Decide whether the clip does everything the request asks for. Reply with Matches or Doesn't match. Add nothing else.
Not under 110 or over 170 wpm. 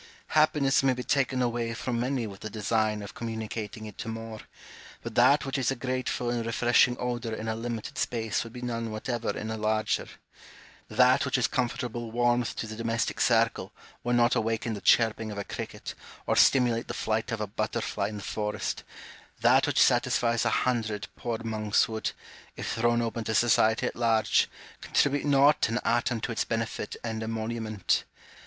Doesn't match